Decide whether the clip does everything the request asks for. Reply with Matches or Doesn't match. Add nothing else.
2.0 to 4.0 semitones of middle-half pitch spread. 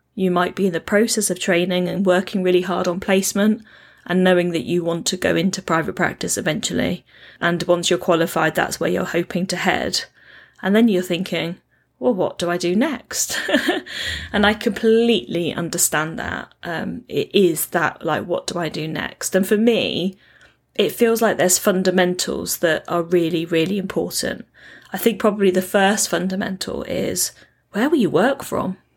Matches